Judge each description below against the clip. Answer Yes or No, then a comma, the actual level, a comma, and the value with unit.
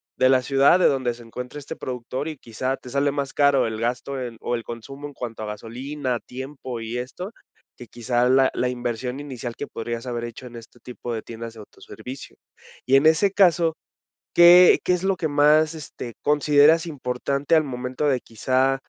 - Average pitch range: Yes, average, 3.2 semitones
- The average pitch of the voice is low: Yes, low, 130 Hz